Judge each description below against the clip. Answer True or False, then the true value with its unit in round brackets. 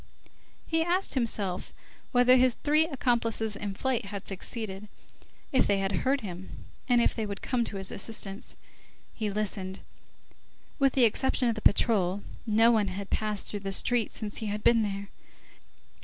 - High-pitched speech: True (215 Hz)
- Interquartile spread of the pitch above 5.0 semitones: False (3.7 semitones)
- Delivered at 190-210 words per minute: False (165 wpm)